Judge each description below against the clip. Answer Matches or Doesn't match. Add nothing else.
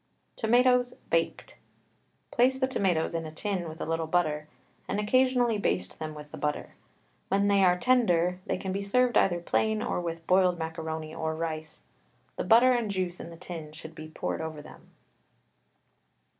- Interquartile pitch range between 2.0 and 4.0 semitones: Doesn't match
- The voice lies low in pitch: Doesn't match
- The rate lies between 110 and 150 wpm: Doesn't match